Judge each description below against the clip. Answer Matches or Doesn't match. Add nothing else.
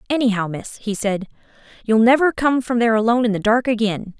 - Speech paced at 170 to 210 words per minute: Matches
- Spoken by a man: Doesn't match